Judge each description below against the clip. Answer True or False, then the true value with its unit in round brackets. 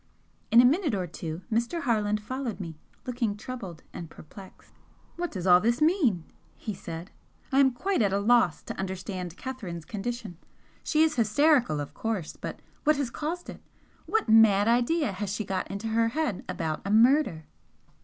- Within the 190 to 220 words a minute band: False (175 wpm)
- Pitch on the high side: True (220 Hz)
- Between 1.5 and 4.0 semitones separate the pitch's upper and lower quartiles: False (5.6 semitones)